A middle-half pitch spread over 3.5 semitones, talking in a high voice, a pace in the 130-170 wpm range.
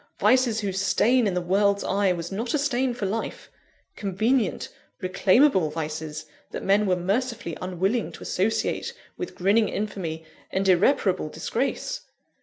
Yes: average, 4.2 semitones; high, 200 Hz; average, 140 wpm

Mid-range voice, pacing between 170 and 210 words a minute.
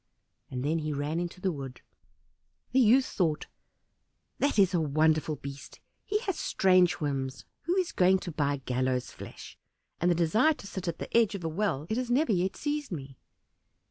Yes: medium, 175 Hz; average, 185 wpm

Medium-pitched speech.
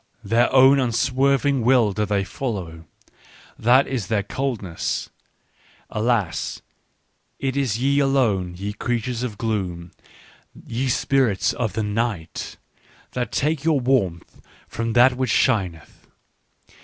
No: low, 115 Hz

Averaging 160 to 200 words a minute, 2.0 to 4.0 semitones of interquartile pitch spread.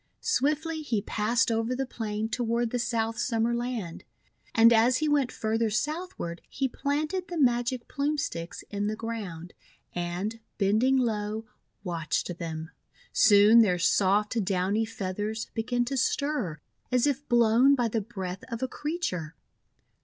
No: average, 145 wpm; average, 3.7 semitones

